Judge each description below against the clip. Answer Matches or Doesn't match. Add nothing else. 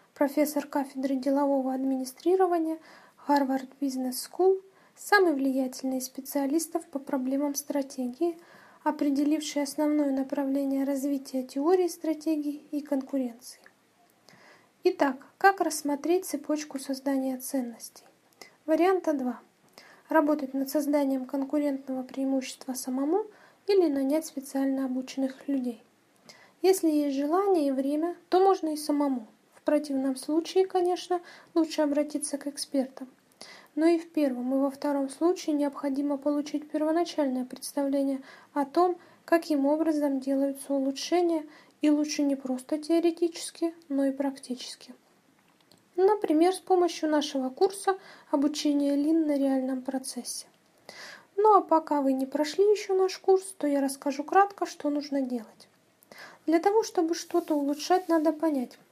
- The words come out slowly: Doesn't match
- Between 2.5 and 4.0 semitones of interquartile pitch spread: Matches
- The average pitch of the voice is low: Doesn't match